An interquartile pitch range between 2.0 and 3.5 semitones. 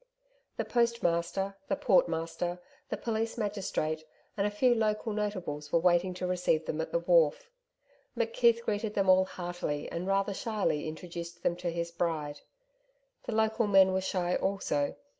No: average, 3.9 semitones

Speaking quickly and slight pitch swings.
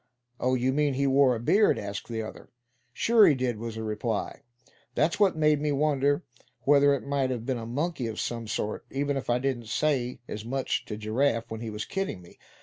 No: fast, 215 wpm; average, 3.8 semitones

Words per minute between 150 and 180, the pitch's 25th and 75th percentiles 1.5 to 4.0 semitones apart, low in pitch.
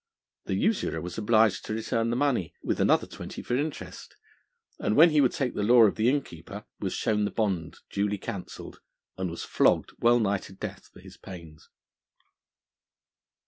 No: average, 170 wpm; average, 4.4 semitones; low, 110 Hz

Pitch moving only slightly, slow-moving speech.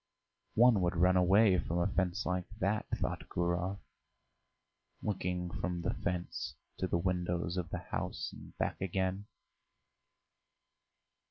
Yes: narrow, 1.5 semitones; slow, 125 wpm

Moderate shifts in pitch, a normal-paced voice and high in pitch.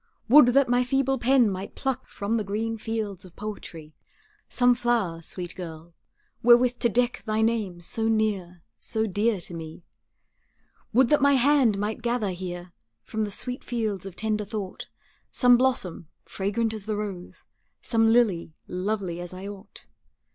Yes: average, 4.3 semitones; average, 160 wpm; high, 215 Hz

